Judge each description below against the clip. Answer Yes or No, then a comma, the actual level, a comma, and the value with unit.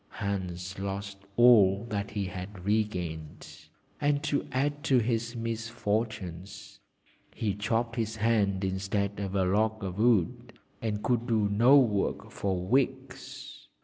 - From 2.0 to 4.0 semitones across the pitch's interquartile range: Yes, average, 3.1 semitones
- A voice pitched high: No, low, 105 Hz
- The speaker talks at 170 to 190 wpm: No, slow, 135 wpm